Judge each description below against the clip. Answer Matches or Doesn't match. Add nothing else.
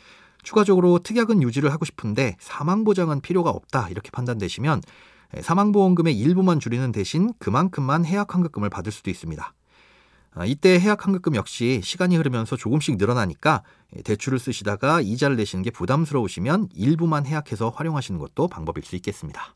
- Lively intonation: Matches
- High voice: Doesn't match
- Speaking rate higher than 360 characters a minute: Matches